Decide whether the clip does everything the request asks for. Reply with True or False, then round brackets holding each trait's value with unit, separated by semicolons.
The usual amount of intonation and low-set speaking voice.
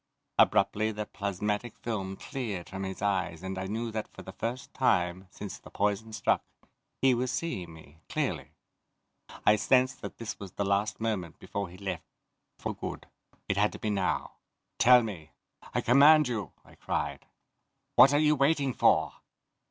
True (4.1 semitones; 105 Hz)